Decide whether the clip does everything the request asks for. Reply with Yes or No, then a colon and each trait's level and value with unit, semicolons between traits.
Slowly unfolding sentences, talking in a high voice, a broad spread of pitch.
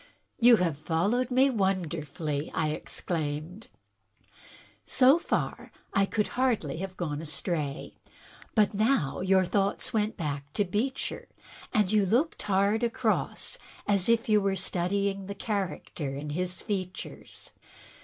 No: slow, 130 wpm; high, 195 Hz; average, 4.8 semitones